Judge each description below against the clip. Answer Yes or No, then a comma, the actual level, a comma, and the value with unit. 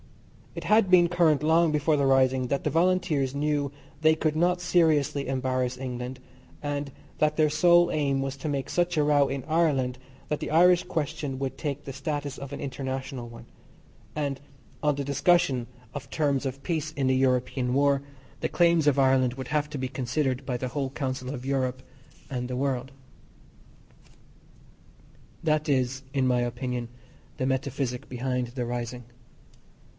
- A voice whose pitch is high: No, medium, 140 Hz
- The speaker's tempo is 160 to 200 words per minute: Yes, average, 165 wpm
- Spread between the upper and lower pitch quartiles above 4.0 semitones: No, average, 2.8 semitones